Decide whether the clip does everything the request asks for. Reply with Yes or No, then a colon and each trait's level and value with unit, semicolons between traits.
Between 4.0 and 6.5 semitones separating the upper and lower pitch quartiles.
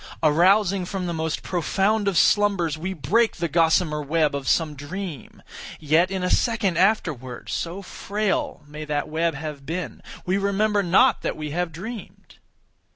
Yes: average, 4.3 semitones